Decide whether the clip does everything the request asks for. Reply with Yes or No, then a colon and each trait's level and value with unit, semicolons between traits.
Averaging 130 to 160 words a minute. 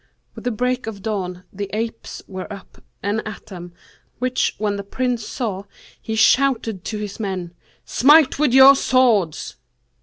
Yes: average, 155 wpm